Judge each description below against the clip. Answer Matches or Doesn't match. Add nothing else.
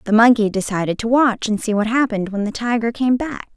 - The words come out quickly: Matches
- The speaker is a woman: Matches